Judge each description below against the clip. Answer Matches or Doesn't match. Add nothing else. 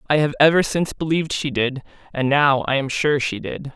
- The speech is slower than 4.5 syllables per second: Doesn't match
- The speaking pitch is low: Doesn't match